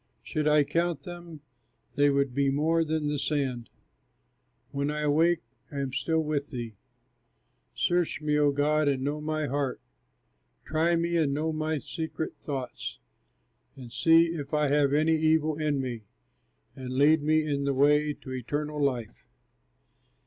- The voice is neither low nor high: Yes, medium, 150 Hz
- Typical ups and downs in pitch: No, narrow, 2.1 semitones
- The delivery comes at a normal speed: Yes, average, 155 wpm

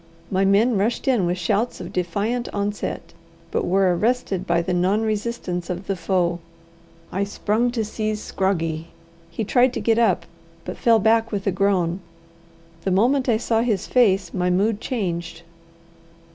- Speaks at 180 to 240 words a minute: No, average, 160 wpm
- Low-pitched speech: No, high, 200 Hz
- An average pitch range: Yes, average, 3.8 semitones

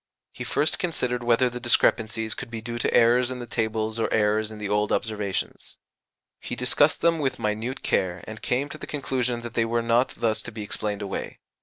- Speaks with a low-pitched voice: Yes, low, 115 Hz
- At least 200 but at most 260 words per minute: Yes, fast, 205 wpm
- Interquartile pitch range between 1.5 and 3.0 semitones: Yes, narrow, 2.4 semitones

